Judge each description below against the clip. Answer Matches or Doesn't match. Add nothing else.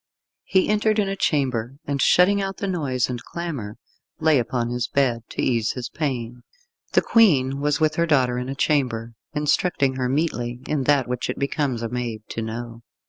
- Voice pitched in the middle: Doesn't match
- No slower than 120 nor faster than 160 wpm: Doesn't match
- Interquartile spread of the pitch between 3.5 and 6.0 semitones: Matches